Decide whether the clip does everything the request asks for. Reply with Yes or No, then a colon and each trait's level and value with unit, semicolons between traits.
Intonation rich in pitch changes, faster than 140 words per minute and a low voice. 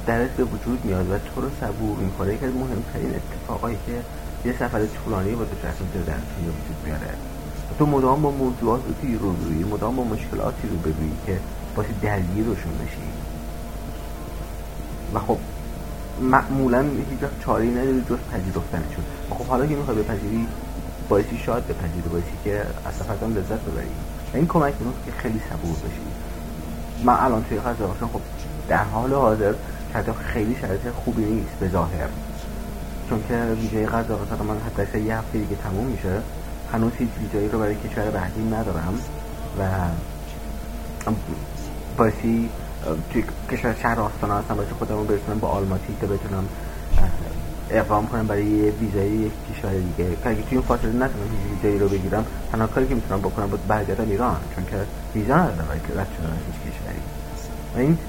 Yes: wide, 6.3 semitones; fast, 155 wpm; low, 100 Hz